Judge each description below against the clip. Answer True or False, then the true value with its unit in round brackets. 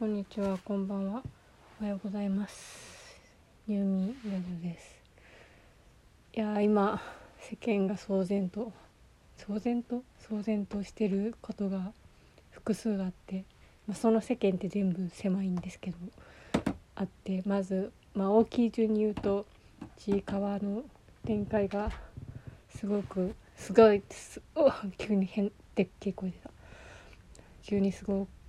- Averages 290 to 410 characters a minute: False (255 characters per minute)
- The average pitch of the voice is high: True (200 Hz)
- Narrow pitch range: True (1.8 semitones)